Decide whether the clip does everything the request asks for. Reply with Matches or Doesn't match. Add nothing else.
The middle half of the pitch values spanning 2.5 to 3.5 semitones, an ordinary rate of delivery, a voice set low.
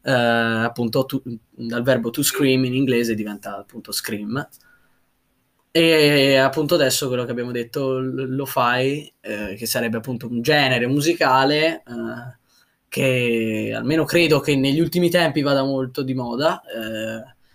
Matches